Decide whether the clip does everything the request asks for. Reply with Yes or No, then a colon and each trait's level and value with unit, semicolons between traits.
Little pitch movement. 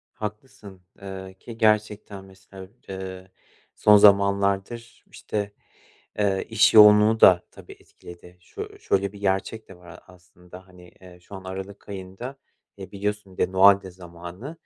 Yes: narrow, 2.1 semitones